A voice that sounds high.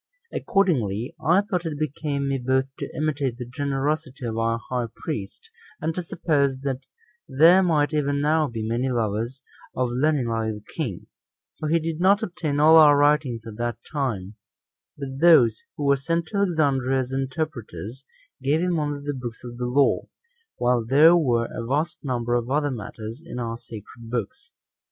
No: low, 135 Hz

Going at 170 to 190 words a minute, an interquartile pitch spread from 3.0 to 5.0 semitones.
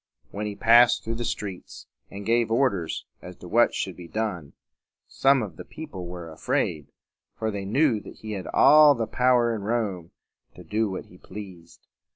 Yes: average, 180 wpm; average, 4.3 semitones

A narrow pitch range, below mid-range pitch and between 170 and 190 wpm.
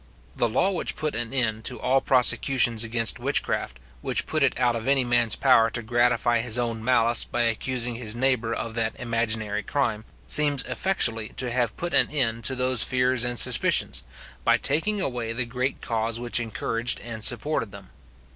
Yes: narrow, 2.1 semitones; low, 120 Hz; average, 180 wpm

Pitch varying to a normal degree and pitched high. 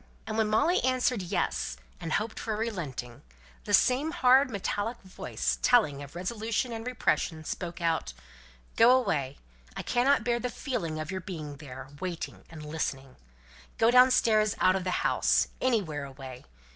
No: wide, 7.5 semitones; high, 200 Hz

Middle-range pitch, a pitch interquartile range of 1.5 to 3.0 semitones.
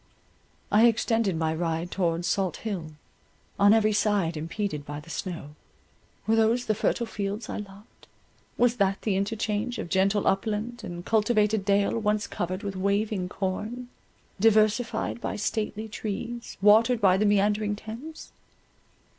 No: high, 205 Hz; narrow, 2.6 semitones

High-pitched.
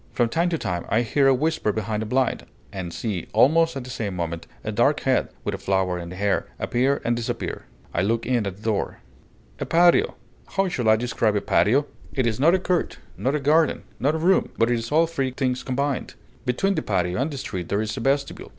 No: low, 125 Hz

